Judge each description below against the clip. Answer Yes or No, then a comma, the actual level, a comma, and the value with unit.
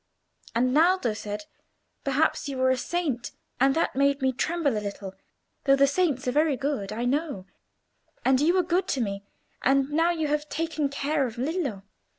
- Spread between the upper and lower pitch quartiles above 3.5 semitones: Yes, average, 4.1 semitones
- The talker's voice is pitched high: Yes, very high, 275 Hz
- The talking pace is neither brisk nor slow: Yes, average, 180 wpm